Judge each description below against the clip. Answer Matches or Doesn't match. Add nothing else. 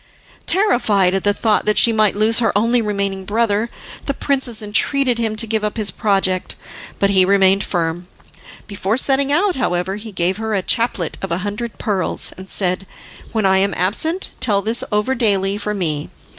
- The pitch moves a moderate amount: Matches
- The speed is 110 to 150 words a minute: Doesn't match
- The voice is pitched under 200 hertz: Doesn't match